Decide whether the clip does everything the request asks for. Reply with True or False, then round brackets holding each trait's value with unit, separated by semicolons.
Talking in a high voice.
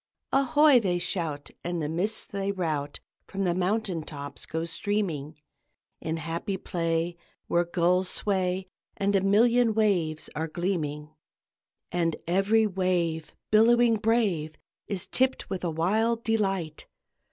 False (180 Hz)